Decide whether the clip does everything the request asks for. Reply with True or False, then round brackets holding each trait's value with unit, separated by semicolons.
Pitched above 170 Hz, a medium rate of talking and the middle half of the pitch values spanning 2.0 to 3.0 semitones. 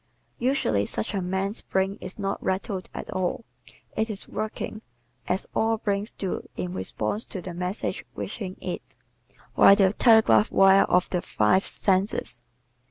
True (190 Hz; 150 wpm; 2.5 semitones)